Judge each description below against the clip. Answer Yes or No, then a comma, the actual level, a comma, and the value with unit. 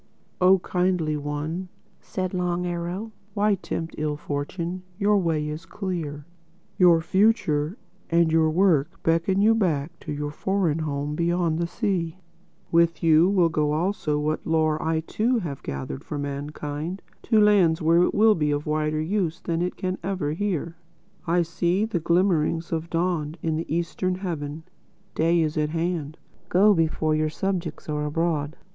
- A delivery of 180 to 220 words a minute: No, average, 155 wpm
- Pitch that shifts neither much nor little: Yes, average, 3.1 semitones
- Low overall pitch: No, medium, 165 Hz